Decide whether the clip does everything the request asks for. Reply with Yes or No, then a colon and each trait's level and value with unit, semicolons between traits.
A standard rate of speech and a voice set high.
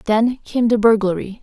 Yes: average, 170 wpm; high, 220 Hz